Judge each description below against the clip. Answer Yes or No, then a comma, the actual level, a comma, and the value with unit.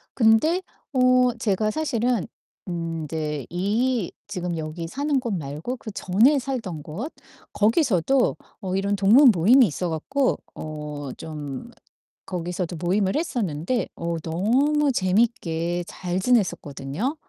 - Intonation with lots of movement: Yes, wide, 6.9 semitones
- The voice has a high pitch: Yes, high, 195 Hz